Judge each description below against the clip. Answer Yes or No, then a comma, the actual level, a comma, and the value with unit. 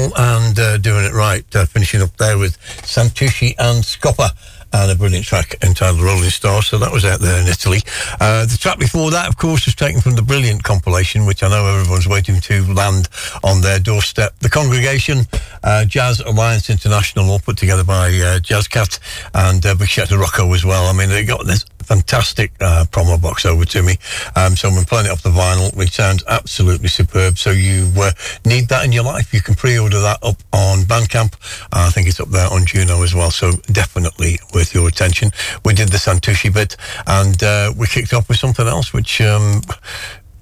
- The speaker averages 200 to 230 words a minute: Yes, fast, 205 wpm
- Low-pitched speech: Yes, low, 100 Hz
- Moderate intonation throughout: Yes, average, 3.2 semitones